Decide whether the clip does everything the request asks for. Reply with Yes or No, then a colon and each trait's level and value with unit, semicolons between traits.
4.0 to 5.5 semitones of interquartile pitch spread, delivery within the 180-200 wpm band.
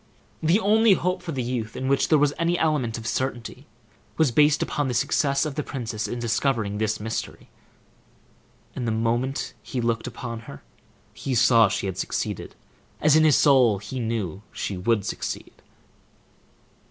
No: average, 4.6 semitones; average, 165 wpm